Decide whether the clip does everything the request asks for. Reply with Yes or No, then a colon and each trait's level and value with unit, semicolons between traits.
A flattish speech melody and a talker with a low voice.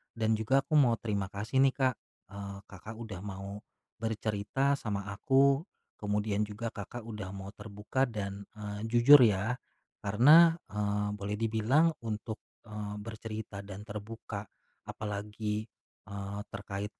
Yes: narrow, 2.2 semitones; low, 105 Hz